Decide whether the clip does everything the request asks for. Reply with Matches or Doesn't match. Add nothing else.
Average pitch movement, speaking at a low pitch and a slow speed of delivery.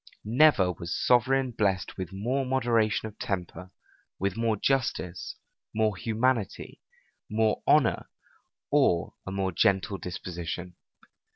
Matches